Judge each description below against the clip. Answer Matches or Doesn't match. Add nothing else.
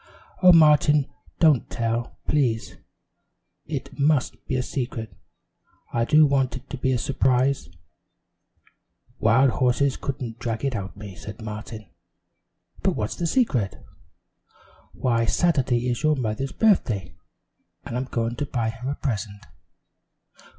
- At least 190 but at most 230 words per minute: Doesn't match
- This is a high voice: Doesn't match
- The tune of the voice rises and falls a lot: Doesn't match